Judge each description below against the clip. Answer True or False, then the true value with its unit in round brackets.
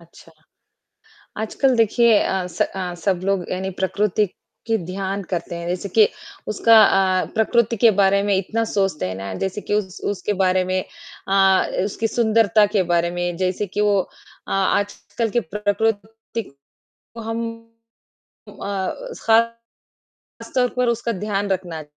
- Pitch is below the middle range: False (200 Hz)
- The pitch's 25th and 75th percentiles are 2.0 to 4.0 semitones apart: True (3.2 semitones)